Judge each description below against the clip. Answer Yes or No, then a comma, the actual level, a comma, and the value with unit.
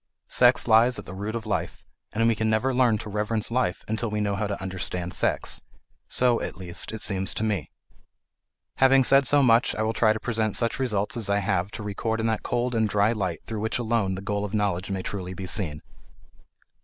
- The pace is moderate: No, fast, 220 wpm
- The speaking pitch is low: Yes, low, 110 Hz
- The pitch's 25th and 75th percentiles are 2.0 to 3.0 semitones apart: Yes, average, 2.7 semitones